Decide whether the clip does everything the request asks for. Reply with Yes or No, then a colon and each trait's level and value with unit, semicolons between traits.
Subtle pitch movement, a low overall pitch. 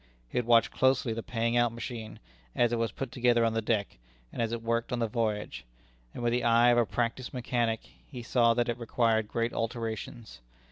Yes: narrow, 1.1 semitones; low, 115 Hz